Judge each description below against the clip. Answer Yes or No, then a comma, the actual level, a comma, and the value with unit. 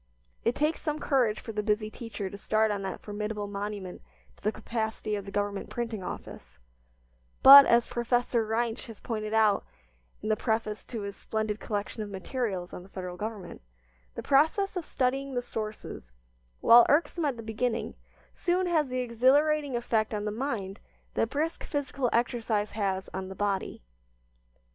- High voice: Yes, high, 220 Hz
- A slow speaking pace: No, average, 165 wpm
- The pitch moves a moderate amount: Yes, average, 3.5 semitones